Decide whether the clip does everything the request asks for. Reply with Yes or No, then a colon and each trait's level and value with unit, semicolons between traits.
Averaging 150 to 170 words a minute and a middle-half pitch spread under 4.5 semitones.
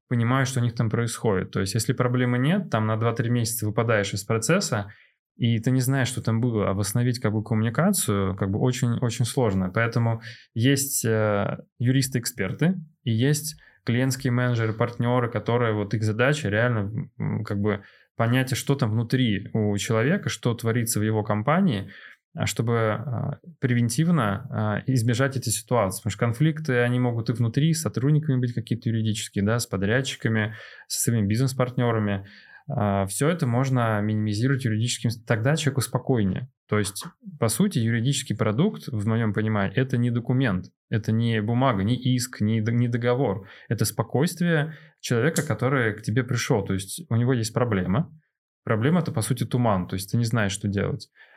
Yes: fast, 160 wpm; average, 3.3 semitones